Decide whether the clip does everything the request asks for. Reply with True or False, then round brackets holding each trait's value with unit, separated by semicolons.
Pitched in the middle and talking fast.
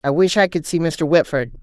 True (160 Hz; 260 wpm)